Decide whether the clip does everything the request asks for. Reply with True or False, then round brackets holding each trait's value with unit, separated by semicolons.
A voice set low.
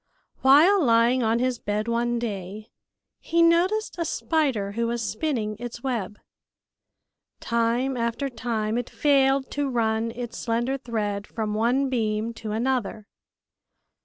False (235 Hz)